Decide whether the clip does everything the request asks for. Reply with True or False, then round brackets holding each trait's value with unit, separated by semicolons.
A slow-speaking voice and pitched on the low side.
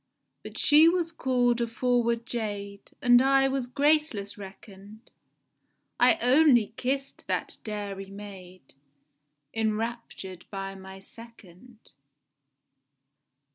False (95 wpm; 230 Hz)